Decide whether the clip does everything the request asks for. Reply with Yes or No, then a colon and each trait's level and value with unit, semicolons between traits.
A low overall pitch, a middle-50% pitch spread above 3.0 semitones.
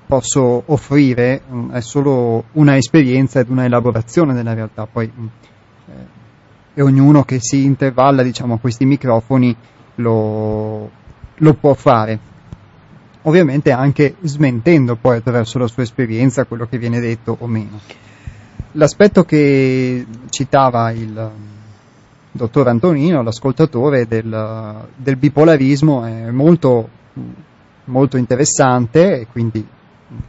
Yes: low, 125 Hz; average, 3.5 semitones